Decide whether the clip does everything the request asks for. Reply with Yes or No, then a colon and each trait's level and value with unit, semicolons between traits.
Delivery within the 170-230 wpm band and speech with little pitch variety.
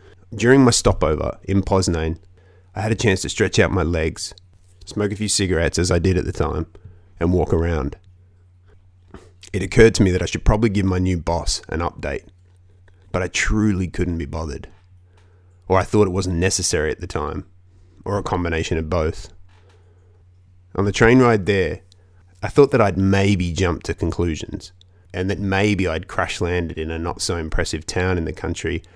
Yes: average, 185 wpm; narrow, 2.0 semitones